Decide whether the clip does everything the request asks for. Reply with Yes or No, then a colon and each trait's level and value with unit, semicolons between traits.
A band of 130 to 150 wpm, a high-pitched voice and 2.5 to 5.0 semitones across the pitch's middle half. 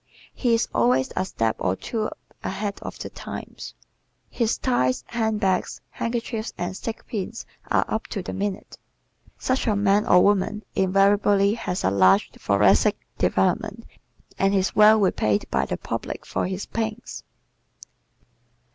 Yes: average, 140 wpm; high, 200 Hz; average, 3.1 semitones